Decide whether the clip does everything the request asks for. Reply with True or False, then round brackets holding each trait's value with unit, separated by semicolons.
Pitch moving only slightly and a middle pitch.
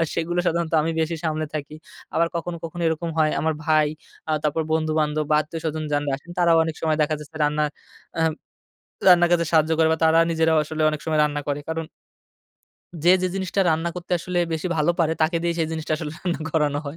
True (1.5 semitones; 160 Hz)